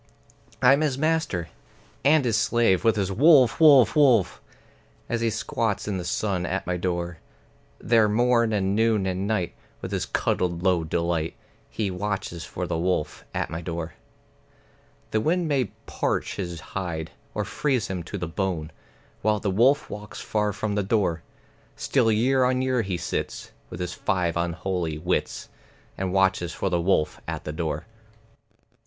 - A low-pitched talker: Yes, very low, 95 Hz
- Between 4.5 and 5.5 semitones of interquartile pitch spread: Yes, average, 4.9 semitones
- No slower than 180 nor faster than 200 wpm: No, average, 160 wpm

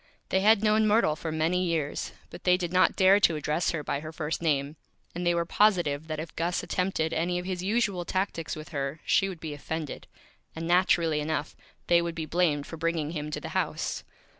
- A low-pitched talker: No, medium, 165 Hz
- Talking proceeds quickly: Yes, fast, 215 wpm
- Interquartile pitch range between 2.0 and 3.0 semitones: Yes, average, 2.7 semitones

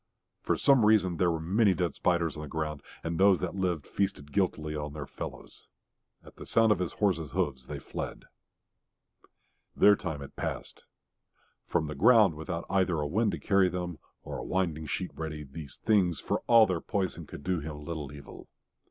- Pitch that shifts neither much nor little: Yes, average, 4.0 semitones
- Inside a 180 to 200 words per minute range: Yes, average, 185 wpm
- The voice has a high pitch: No, very low, 85 Hz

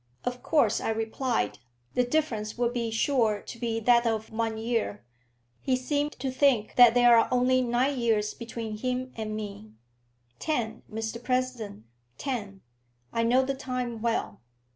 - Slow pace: No, average, 155 wpm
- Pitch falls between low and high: No, high, 235 Hz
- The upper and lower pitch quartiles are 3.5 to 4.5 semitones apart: No, narrow, 2.4 semitones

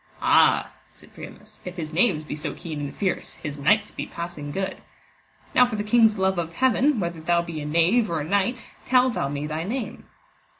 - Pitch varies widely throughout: Yes, wide, 5.7 semitones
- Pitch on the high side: No, medium, 175 Hz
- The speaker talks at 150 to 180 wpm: No, fast, 205 wpm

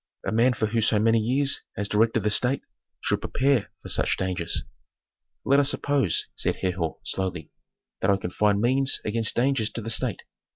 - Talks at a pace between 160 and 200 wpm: Yes, average, 180 wpm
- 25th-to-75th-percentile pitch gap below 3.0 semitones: No, average, 4.2 semitones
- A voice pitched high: No, low, 110 Hz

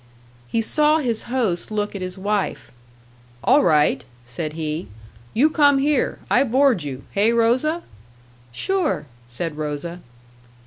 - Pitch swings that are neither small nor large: No, wide, 8.9 semitones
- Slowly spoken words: Yes, slow, 130 wpm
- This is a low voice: No, high, 215 Hz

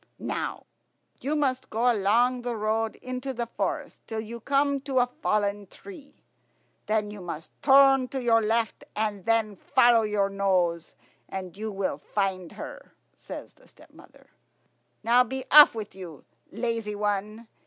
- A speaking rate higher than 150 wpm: No, average, 145 wpm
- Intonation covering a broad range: No, average, 3.6 semitones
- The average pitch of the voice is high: Yes, high, 225 Hz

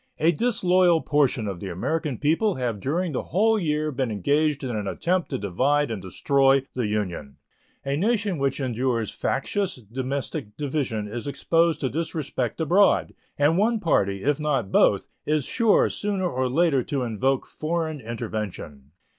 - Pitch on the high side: No, medium, 140 Hz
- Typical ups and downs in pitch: No, wide, 6.0 semitones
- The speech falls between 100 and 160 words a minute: Yes, average, 155 wpm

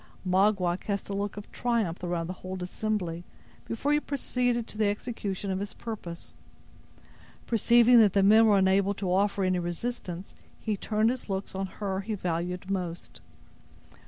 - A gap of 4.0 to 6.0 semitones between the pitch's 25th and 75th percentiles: No, average, 3.1 semitones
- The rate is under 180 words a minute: Yes, average, 160 wpm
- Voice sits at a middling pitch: No, high, 200 Hz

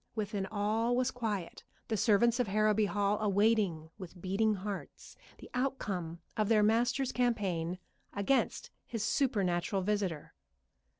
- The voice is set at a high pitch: Yes, high, 210 Hz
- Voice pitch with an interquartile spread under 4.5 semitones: Yes, average, 3.0 semitones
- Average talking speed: No, slow, 125 wpm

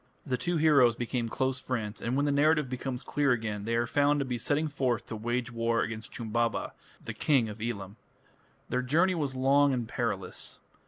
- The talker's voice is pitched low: Yes, low, 125 Hz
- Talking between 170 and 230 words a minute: Yes, average, 195 wpm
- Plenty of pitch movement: No, average, 3.5 semitones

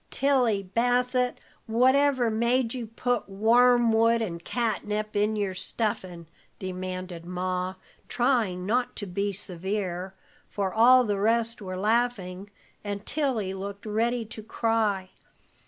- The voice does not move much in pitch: No, average, 4.0 semitones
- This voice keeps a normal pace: No, slow, 120 wpm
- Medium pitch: No, high, 215 Hz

